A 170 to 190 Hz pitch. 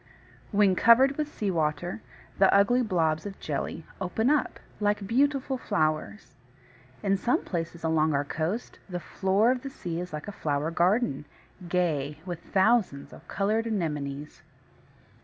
Yes: medium, 185 Hz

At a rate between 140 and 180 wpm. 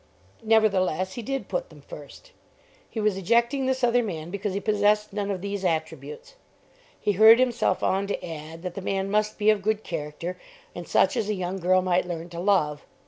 No: average, 195 wpm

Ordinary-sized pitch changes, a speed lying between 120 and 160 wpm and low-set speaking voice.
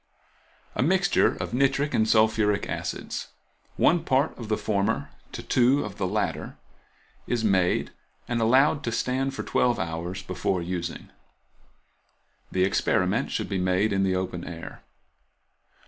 No: wide, 5.7 semitones; average, 140 wpm; low, 110 Hz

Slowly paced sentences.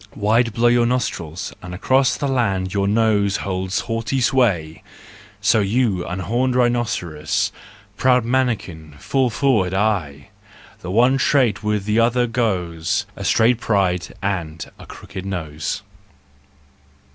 Yes: slow, 125 wpm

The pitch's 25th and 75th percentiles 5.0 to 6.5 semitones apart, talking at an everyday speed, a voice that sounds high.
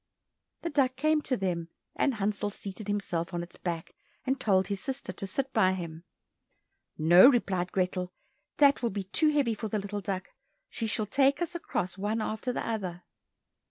Yes: wide, 5.6 semitones; average, 180 wpm; high, 205 Hz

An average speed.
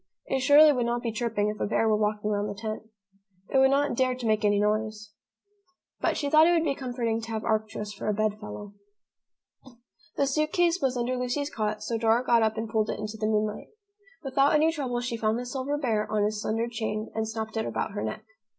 No: fast, 230 wpm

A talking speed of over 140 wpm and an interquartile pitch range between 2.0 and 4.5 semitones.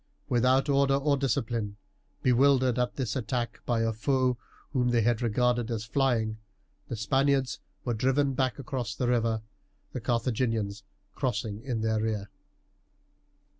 No: slow, 135 wpm; average, 2.9 semitones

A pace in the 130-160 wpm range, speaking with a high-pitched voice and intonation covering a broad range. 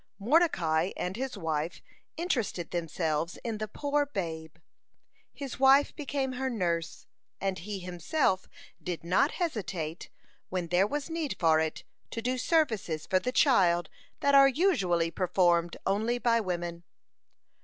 Yes: slow, 135 wpm; high, 195 Hz; wide, 7.7 semitones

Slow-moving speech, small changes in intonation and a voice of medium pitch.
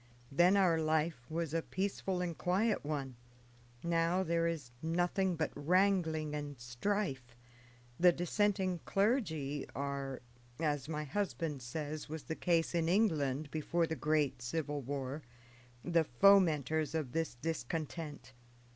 No: slow, 130 wpm; average, 3.5 semitones; medium, 160 Hz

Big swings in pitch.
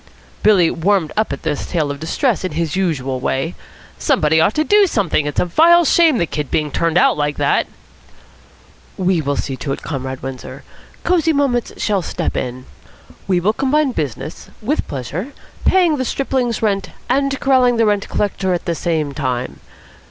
Yes: wide, 9.0 semitones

